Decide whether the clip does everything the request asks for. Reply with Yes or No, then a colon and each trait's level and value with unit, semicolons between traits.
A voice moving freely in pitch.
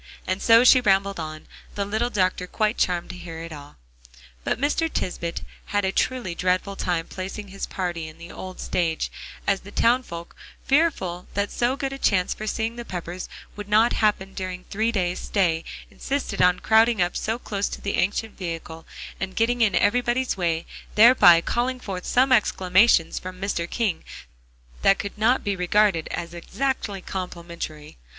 No: average, 4.2 semitones